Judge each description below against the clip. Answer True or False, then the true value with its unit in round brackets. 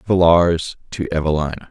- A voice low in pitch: True (85 Hz)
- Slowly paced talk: True (105 wpm)